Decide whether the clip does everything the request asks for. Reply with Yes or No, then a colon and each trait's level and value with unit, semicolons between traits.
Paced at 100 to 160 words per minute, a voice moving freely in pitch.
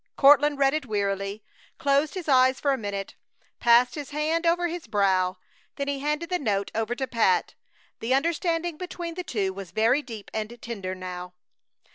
No: average, 175 wpm; wide, 6.9 semitones